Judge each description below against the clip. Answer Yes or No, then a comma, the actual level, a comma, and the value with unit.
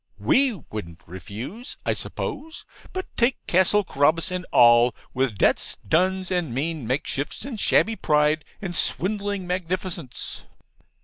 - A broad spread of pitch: Yes, wide, 7.0 semitones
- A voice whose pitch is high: No, medium, 175 Hz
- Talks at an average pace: No, slow, 125 wpm